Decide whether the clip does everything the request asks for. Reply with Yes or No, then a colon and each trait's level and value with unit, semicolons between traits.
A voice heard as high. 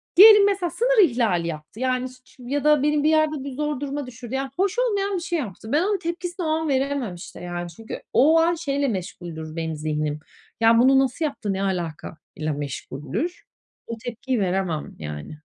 Yes: very high, 260 Hz